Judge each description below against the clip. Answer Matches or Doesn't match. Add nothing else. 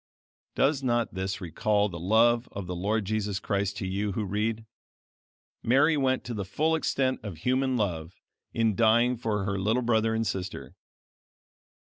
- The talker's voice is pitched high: Doesn't match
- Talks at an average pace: Matches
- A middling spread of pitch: Matches